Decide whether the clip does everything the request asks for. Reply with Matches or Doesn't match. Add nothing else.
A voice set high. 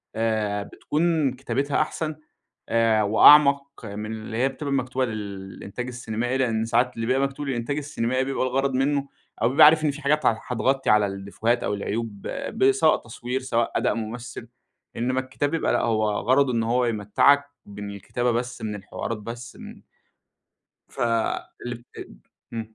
Doesn't match